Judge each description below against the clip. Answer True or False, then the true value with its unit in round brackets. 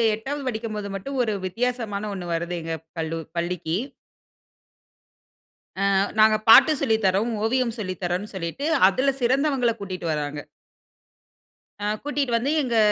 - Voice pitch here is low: False (215 Hz)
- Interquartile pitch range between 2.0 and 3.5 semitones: False (5.6 semitones)